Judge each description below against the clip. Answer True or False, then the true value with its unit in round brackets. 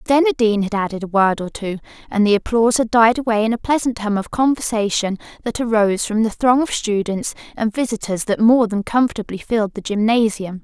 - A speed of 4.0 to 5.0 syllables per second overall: False (5.8 syllables/s)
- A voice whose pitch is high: True (220 Hz)